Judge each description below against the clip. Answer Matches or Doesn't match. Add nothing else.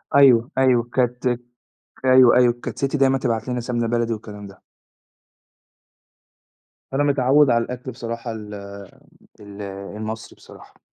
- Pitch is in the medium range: Doesn't match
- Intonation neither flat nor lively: Doesn't match